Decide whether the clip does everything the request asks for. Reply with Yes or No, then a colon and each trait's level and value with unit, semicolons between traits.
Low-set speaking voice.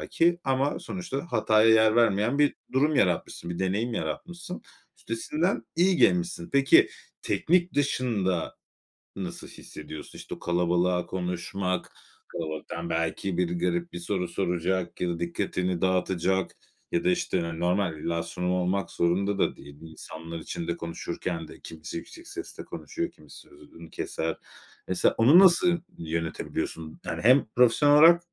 Yes: very low, 95 Hz